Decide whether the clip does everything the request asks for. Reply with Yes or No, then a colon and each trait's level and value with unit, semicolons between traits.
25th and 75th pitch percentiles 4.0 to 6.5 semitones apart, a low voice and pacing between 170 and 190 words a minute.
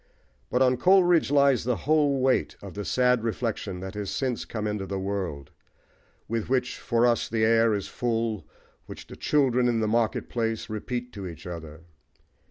No: average, 3.6 semitones; low, 115 Hz; average, 180 wpm